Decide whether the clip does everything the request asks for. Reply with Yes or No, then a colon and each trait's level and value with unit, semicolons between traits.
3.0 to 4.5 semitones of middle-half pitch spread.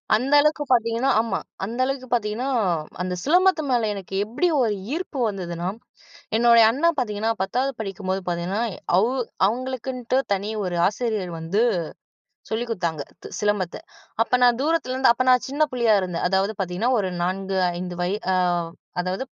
No: average, 4.9 semitones